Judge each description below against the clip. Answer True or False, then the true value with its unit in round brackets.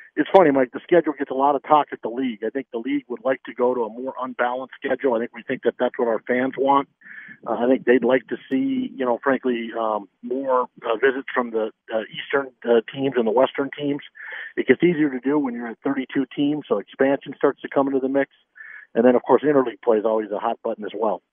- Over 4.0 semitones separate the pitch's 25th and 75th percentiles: False (2.4 semitones)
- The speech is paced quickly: True (255 wpm)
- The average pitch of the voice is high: False (130 Hz)